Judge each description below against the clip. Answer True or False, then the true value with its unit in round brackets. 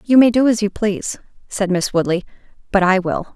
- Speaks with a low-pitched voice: False (205 Hz)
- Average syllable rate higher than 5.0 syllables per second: True (5.8 syllables/s)